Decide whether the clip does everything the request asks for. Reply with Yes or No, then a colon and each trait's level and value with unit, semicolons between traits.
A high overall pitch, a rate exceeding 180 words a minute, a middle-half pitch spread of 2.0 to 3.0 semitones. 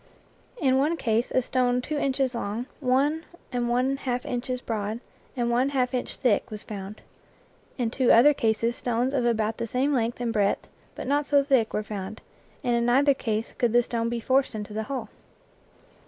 Yes: high, 245 Hz; average, 190 wpm; average, 2.7 semitones